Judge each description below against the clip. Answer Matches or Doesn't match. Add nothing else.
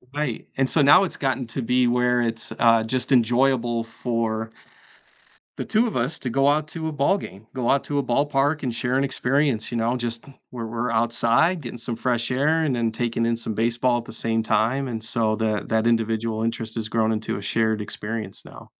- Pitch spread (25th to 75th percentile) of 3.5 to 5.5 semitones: Doesn't match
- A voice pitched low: Matches